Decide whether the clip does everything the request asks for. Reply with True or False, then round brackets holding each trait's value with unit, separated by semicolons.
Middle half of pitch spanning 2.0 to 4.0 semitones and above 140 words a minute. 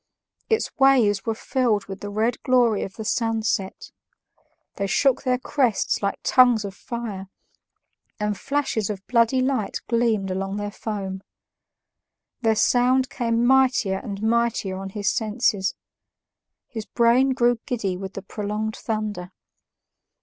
False (3.5 semitones; 135 wpm)